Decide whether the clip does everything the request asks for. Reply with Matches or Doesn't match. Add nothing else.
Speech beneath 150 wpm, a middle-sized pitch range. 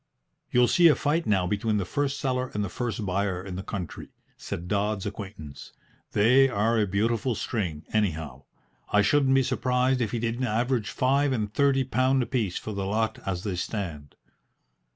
Doesn't match